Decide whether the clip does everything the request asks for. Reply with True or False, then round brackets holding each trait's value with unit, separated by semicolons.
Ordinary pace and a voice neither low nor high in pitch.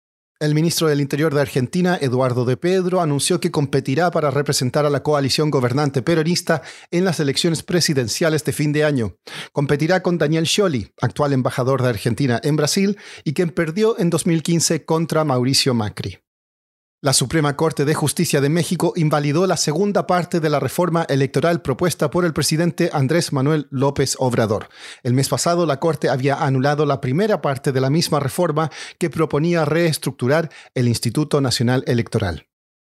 True (160 wpm; 150 Hz)